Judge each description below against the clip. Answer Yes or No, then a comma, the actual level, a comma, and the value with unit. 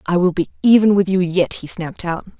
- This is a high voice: No, medium, 180 Hz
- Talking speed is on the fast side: Yes, fast, 250 wpm